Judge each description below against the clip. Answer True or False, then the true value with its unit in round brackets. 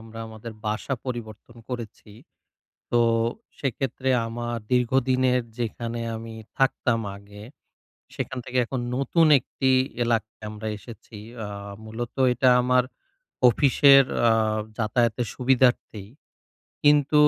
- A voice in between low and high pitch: False (120 Hz)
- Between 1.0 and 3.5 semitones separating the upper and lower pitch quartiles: True (2.6 semitones)